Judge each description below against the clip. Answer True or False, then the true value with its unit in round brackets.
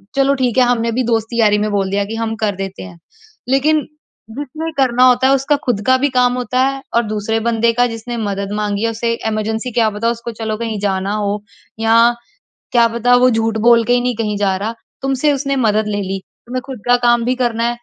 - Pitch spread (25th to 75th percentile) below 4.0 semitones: True (2.9 semitones)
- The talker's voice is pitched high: True (230 Hz)